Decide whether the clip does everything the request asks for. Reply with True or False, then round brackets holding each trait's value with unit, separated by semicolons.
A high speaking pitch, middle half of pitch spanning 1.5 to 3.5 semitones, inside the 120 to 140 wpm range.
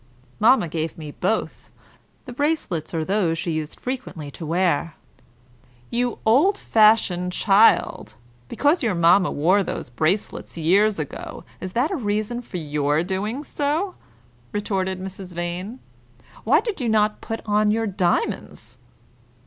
False (195 Hz; 4.9 semitones; 135 wpm)